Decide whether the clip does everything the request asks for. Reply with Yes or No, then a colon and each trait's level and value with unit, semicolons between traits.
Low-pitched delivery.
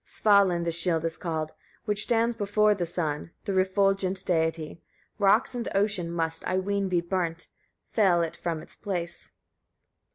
No: medium, 185 Hz